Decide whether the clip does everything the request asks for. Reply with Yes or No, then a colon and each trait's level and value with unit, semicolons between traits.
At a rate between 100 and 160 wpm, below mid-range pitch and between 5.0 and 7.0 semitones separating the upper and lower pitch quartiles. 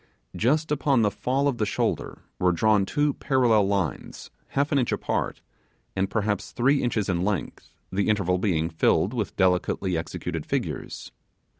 Yes: average, 155 wpm; low, 105 Hz; wide, 5.4 semitones